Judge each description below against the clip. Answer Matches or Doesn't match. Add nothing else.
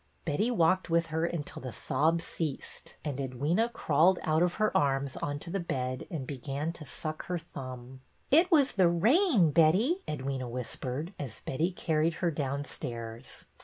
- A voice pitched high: Doesn't match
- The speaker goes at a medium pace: Matches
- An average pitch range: Matches